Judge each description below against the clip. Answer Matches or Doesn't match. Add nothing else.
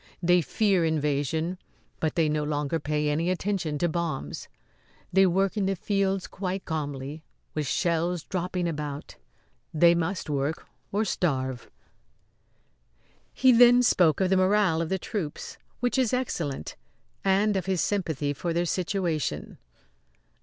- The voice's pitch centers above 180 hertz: Doesn't match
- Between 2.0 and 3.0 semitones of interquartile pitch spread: Doesn't match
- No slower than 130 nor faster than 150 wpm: Matches